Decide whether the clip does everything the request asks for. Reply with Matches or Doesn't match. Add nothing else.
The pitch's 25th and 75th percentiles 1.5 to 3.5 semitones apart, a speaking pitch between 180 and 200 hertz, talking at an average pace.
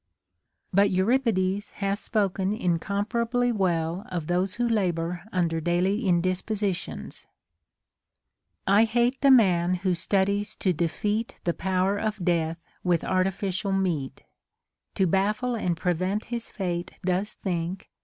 Doesn't match